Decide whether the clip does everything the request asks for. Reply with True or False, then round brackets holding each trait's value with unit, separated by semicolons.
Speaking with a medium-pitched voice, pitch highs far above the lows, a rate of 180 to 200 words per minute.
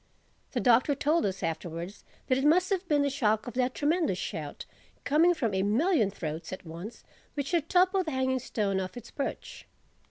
False (260 Hz; 7.8 semitones; 190 wpm)